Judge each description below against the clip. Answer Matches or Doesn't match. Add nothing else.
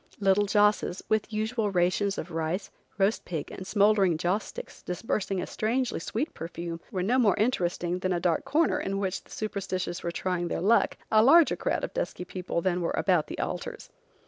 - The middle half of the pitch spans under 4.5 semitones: Matches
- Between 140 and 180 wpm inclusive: Doesn't match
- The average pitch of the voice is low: Doesn't match